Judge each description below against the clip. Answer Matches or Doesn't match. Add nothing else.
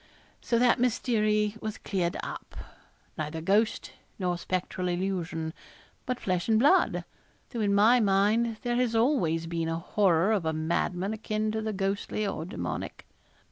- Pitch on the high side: Matches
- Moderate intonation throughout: Matches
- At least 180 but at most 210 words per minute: Doesn't match